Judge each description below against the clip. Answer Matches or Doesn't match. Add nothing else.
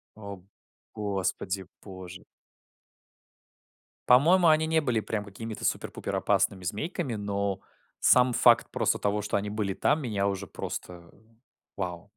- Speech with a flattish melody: Doesn't match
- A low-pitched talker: Matches